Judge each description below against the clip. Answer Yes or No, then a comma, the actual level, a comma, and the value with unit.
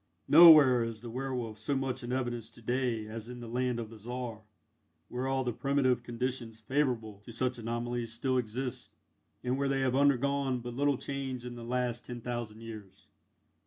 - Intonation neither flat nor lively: No, narrow, 2.2 semitones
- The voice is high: No, low, 125 Hz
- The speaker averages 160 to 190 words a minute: Yes, average, 185 wpm